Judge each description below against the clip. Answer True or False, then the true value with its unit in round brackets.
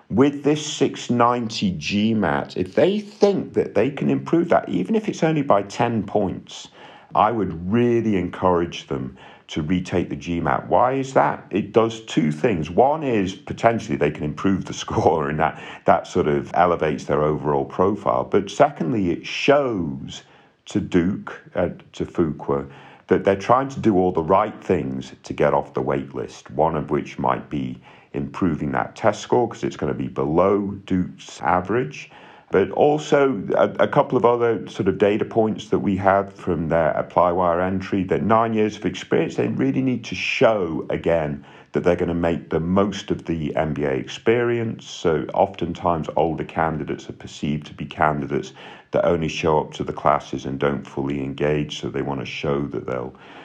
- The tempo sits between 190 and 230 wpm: False (180 wpm)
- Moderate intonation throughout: False (7.8 semitones)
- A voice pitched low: True (90 Hz)